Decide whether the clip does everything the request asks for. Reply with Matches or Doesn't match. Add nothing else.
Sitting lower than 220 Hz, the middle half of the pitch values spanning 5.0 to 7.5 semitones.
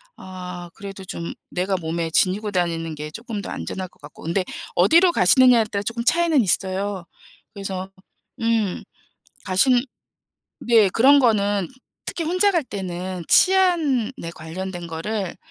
Doesn't match